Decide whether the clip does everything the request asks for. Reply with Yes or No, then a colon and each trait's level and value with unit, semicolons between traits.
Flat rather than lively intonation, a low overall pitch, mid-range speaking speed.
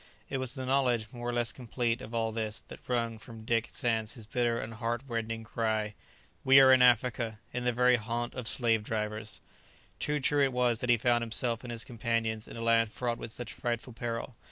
No: narrow, 1.6 semitones; low, 115 Hz; fast, 215 wpm